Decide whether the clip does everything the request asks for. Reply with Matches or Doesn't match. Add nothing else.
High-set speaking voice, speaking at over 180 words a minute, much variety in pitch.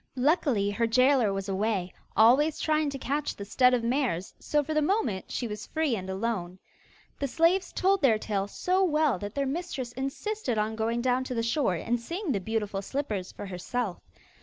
Matches